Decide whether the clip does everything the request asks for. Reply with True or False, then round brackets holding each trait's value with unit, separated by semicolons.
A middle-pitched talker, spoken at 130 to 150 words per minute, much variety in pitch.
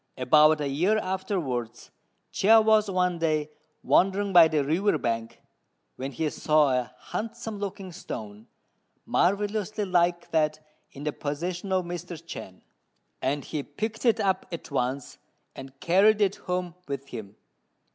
True (170 Hz; 140 wpm; 5.7 semitones)